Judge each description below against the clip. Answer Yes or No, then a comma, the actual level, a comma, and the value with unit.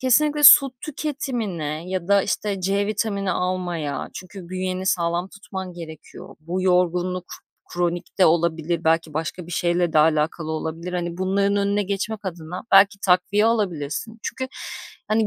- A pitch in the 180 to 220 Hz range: Yes, medium, 185 Hz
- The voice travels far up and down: No, average, 2.9 semitones